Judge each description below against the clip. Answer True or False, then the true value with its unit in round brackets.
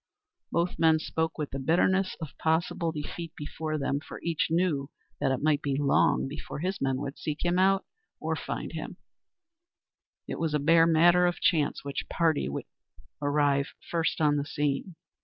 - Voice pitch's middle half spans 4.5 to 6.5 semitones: False (2.8 semitones)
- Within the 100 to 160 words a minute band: False (175 wpm)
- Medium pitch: True (155 Hz)